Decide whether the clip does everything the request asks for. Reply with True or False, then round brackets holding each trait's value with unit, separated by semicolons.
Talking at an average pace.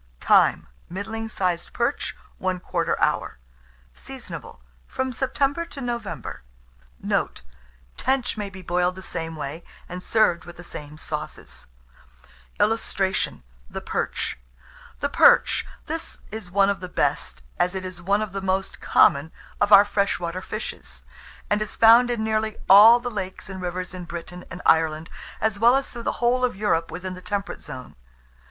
True (160 wpm)